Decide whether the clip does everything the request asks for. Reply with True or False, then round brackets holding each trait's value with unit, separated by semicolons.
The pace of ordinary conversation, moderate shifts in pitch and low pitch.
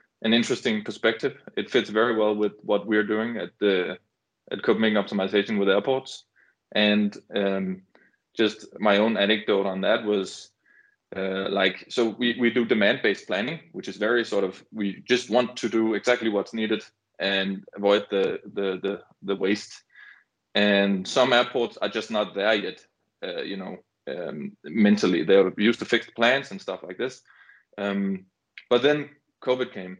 True (165 wpm; 3.5 semitones; 105 Hz)